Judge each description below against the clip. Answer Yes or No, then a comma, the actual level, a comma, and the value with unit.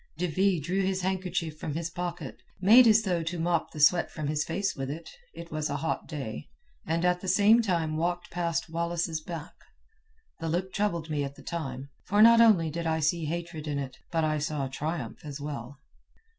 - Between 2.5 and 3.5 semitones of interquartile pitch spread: Yes, average, 2.8 semitones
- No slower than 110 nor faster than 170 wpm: No, fast, 205 wpm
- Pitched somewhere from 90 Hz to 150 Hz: No, medium, 165 Hz